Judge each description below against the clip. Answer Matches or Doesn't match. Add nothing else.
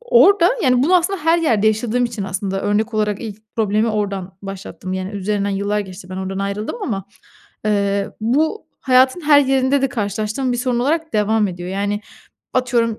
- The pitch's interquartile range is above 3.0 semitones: Matches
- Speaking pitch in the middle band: Doesn't match